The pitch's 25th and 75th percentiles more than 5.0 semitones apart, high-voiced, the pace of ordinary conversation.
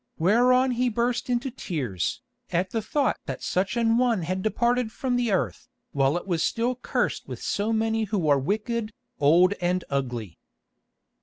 Yes: wide, 5.6 semitones; high, 215 Hz; average, 165 wpm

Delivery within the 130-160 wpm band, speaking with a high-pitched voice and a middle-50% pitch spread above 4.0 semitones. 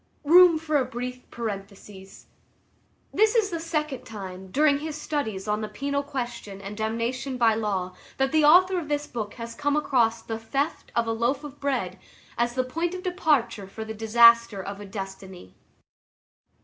No: average, 175 wpm; high, 240 Hz; wide, 5.5 semitones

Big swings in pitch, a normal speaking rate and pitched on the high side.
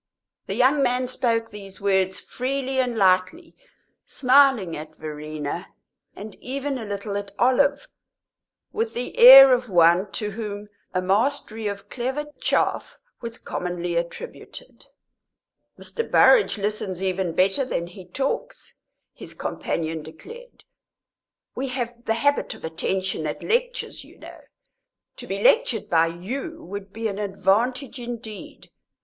No: wide, 5.9 semitones; slow, 130 wpm; high, 220 Hz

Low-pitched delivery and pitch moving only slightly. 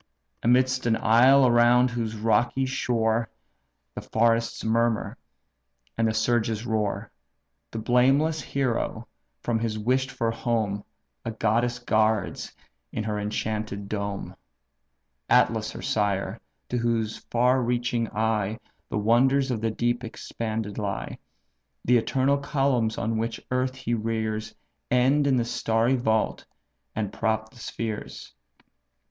Yes: low, 115 Hz; narrow, 2.1 semitones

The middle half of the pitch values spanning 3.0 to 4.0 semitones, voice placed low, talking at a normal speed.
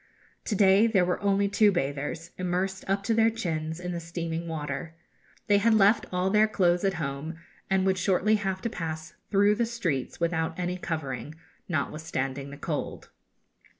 No: average, 3.7 semitones; medium, 180 Hz; average, 170 wpm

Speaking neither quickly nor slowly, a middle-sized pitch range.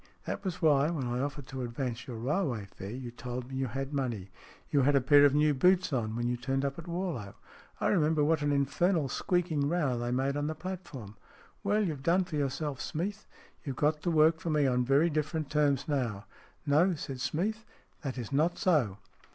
No: fast, 215 wpm; average, 4.1 semitones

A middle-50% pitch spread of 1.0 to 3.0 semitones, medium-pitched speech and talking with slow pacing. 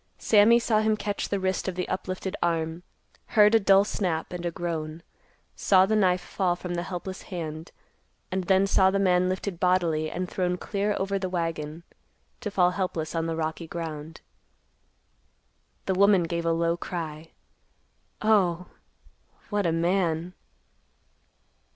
No: average, 2.7 semitones; medium, 180 Hz; average, 150 wpm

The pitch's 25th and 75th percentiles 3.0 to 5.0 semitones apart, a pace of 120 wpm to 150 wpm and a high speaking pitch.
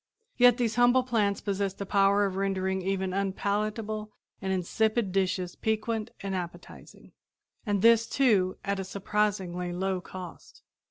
No: narrow, 2.4 semitones; average, 140 wpm; high, 200 Hz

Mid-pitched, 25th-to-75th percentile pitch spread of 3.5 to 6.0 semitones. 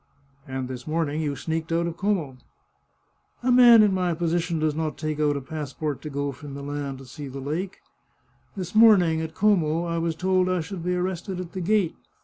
Yes: medium, 160 Hz; average, 3.9 semitones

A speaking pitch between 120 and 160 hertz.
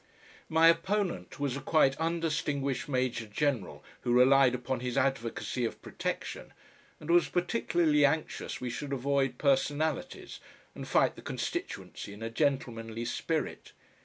Yes: medium, 140 Hz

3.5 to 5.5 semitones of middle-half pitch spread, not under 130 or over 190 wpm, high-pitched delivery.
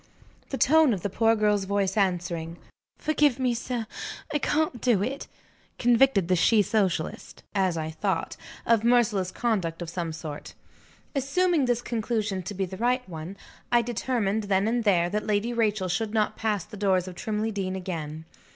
Yes: average, 4.4 semitones; average, 170 wpm; high, 210 Hz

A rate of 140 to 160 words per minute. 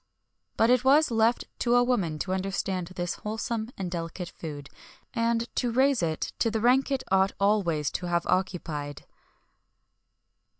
Yes: average, 155 wpm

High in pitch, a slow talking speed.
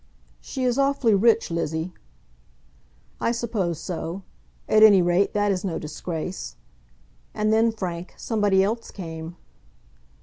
Yes: high, 195 Hz; slow, 125 wpm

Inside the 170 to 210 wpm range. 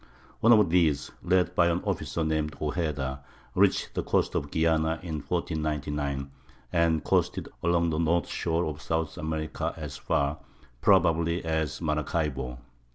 No: average, 140 wpm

